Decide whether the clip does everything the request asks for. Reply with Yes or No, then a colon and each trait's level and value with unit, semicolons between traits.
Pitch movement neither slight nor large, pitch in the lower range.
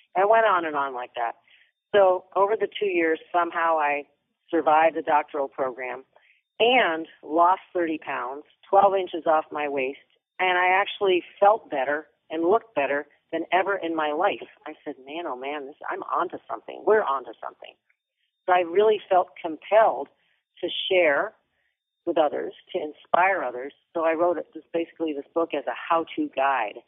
No: average, 3.6 semitones; medium, 165 Hz